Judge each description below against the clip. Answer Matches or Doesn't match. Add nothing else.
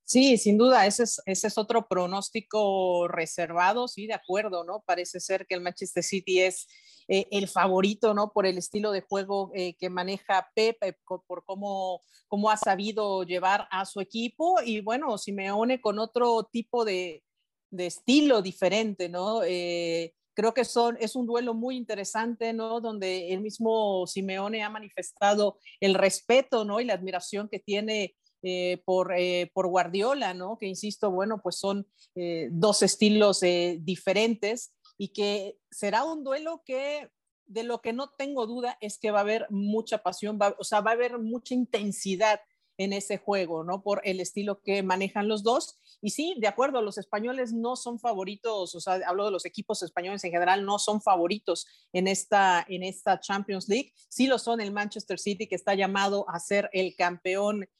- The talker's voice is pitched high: Matches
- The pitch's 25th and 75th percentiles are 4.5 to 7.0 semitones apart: Doesn't match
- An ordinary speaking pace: Matches